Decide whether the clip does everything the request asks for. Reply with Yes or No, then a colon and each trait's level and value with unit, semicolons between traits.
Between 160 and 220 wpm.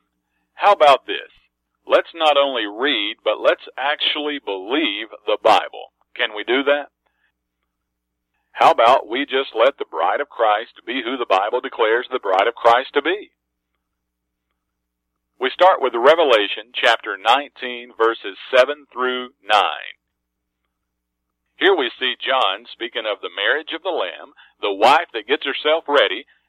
No: average, 145 wpm